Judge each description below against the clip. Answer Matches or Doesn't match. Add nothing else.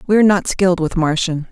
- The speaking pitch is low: Doesn't match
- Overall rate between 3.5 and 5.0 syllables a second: Doesn't match